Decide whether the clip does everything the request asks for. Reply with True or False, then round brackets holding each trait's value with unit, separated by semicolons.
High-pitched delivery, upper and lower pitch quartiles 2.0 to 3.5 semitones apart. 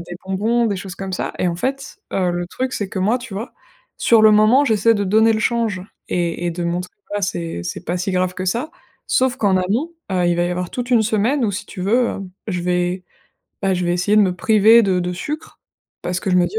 False (195 Hz; 4.1 semitones)